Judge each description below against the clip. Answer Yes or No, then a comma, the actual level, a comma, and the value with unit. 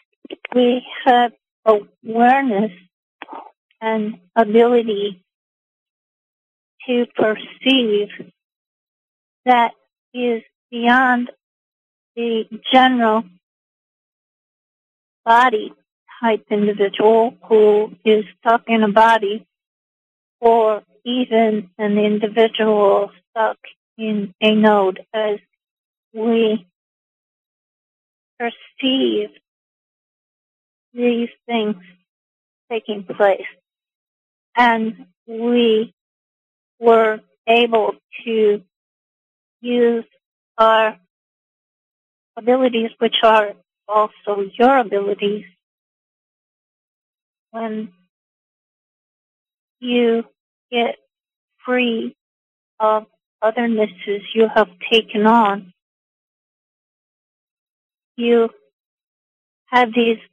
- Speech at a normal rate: No, slow, 60 wpm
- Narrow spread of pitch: Yes, narrow, 2.1 semitones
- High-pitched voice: Yes, high, 225 Hz